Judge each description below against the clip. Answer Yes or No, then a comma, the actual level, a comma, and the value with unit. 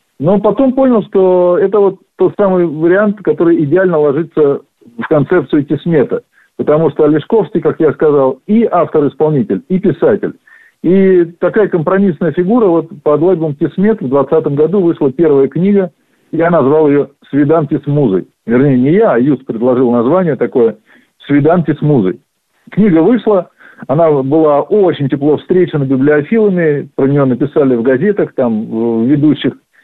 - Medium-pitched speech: Yes, medium, 160 Hz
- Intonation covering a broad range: No, average, 4.7 semitones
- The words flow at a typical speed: Yes, average, 145 wpm